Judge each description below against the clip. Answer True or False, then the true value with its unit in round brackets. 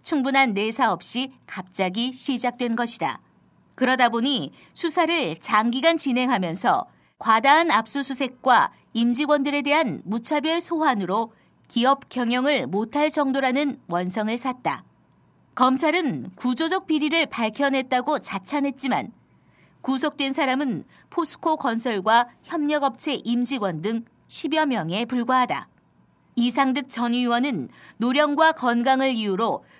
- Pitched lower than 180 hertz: False (260 Hz)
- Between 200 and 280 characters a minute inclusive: True (265 characters per minute)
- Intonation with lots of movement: False (3.6 semitones)